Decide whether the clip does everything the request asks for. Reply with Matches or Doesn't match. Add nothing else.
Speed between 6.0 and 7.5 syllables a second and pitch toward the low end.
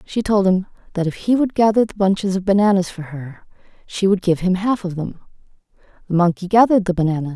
Doesn't match